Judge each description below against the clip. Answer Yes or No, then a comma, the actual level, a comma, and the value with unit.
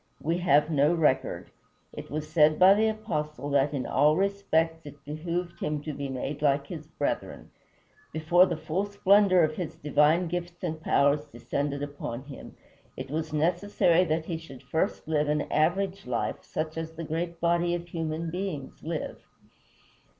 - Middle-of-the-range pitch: Yes, medium, 160 Hz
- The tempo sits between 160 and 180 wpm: Yes, average, 165 wpm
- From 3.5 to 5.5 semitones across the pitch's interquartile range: No, average, 2.8 semitones